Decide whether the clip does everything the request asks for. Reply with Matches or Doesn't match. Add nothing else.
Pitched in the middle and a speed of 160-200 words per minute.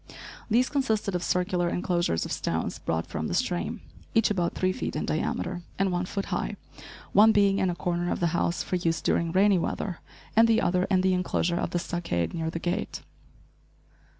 Matches